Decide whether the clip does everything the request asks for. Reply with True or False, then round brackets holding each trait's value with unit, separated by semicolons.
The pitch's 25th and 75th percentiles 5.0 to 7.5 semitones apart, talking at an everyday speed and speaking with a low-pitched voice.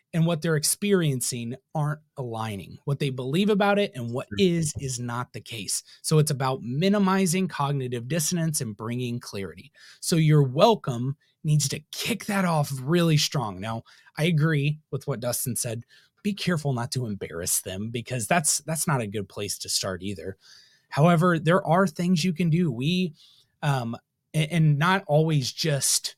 False (5.5 semitones; 170 wpm; 145 Hz)